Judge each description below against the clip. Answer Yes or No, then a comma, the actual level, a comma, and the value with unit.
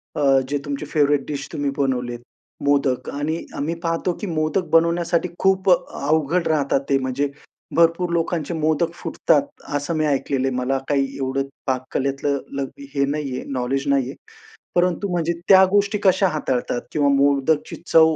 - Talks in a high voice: No, medium, 145 Hz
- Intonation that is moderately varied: Yes, average, 3.4 semitones